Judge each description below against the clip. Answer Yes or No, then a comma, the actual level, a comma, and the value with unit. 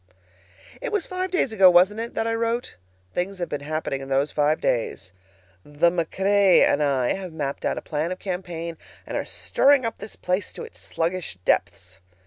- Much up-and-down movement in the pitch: Yes, wide, 5.9 semitones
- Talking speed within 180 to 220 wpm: Yes, average, 190 wpm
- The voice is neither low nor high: Yes, medium, 175 Hz